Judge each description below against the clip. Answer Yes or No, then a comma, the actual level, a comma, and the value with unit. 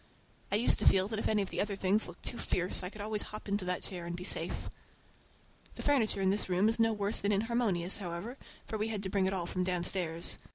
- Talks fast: Yes, fast, 250 wpm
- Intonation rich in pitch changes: No, average, 2.9 semitones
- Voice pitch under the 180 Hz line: No, high, 200 Hz